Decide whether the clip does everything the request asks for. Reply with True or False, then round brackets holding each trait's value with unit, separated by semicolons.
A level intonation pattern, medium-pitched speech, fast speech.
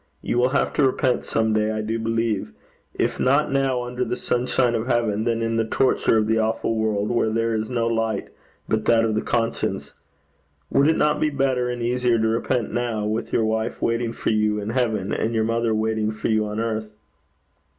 False (1.9 semitones; 115 Hz; 210 wpm)